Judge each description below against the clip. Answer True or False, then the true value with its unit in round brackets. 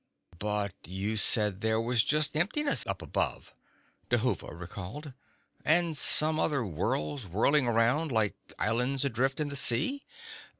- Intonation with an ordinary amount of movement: False (5.9 semitones)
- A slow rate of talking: True (130 wpm)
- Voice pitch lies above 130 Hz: False (120 Hz)